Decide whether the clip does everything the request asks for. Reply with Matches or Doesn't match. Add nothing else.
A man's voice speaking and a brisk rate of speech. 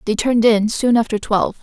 Doesn't match